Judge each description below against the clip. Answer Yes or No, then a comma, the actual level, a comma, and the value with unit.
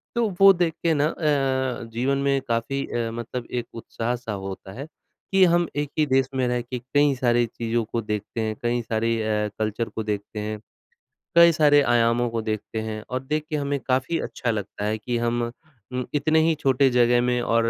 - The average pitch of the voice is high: No, low, 120 Hz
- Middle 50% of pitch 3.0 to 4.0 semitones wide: Yes, average, 3.4 semitones